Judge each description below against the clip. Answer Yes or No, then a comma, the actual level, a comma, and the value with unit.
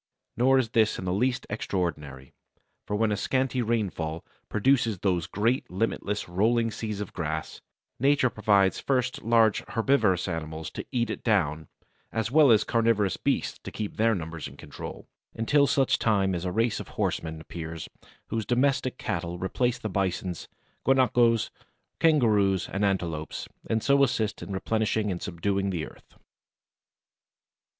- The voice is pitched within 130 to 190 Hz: No, low, 105 Hz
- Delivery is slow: No, average, 150 wpm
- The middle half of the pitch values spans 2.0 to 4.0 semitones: No, average, 4.7 semitones